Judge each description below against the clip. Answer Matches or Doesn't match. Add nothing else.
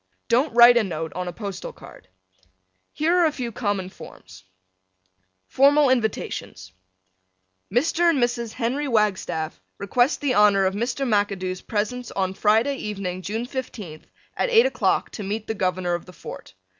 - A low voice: Doesn't match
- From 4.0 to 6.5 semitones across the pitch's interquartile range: Matches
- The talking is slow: Doesn't match